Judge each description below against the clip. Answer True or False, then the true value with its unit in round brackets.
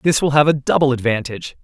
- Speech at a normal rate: False (220 wpm)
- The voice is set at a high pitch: False (135 Hz)